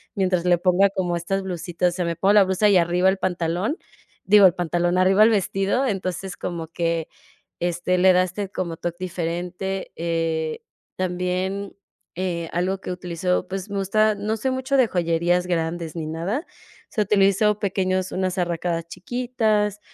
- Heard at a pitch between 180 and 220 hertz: Yes, medium, 185 Hz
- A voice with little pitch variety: Yes, narrow, 2.2 semitones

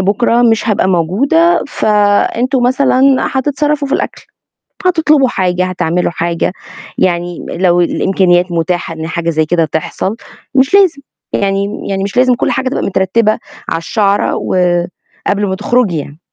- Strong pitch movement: Yes, wide, 6.3 semitones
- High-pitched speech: Yes, high, 200 Hz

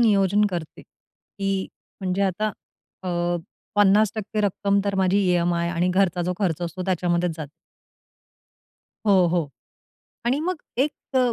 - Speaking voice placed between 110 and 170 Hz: No, high, 190 Hz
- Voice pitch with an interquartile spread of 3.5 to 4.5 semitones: No, average, 2.7 semitones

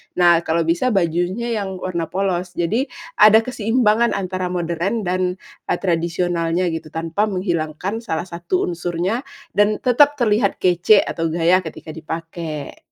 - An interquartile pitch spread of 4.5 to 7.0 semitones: No, average, 3.7 semitones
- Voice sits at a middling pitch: Yes, medium, 180 Hz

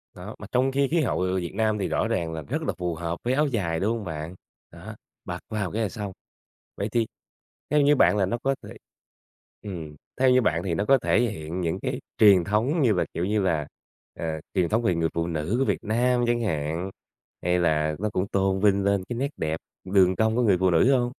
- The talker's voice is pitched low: Yes, low, 100 Hz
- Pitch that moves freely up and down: Yes, wide, 5.7 semitones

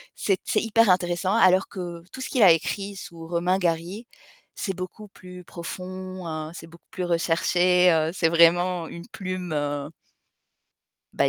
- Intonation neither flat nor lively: No, narrow, 1.9 semitones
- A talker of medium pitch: Yes, medium, 180 Hz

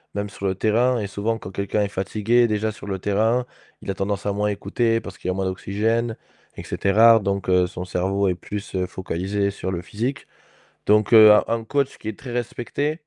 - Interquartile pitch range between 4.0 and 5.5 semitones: No, average, 2.7 semitones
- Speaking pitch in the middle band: No, low, 105 Hz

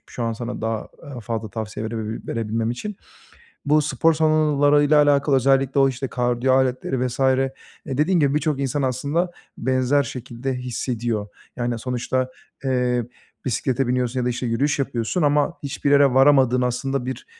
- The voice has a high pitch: No, low, 130 Hz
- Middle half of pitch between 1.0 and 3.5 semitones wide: Yes, average, 2.7 semitones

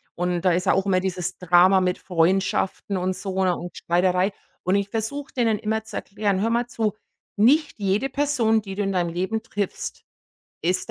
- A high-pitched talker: Yes, high, 195 Hz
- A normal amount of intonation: Yes, average, 3.3 semitones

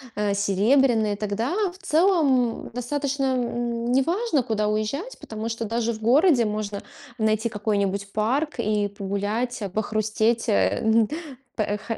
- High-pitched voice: Yes, high, 225 Hz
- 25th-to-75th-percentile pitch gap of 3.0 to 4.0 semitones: Yes, average, 3.4 semitones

